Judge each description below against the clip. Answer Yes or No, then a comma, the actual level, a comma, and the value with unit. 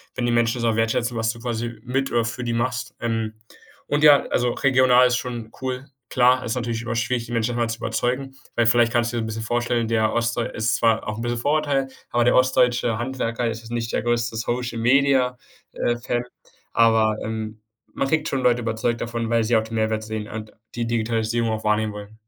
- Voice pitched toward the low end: Yes, low, 120 Hz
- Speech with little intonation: Yes, narrow, 1.6 semitones